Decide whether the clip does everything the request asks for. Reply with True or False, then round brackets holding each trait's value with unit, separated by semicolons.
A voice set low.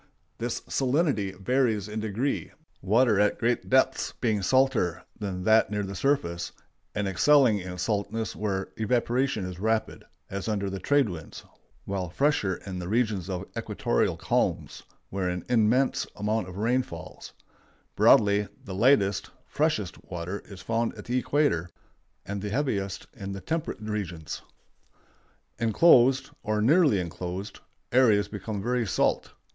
True (105 Hz)